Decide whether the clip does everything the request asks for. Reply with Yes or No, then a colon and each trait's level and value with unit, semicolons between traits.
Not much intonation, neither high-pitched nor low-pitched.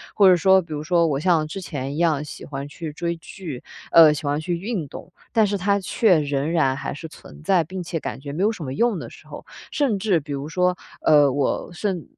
No: average, 4.2 semitones; medium, 165 Hz